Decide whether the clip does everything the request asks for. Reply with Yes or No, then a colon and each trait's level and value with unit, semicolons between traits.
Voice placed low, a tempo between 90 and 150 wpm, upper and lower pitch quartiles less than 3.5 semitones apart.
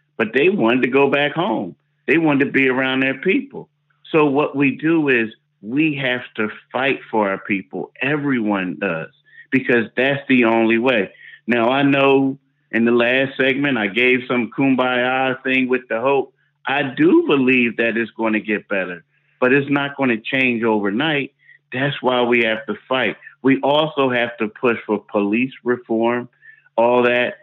No: low, 130 Hz; average, 175 wpm; average, 3.1 semitones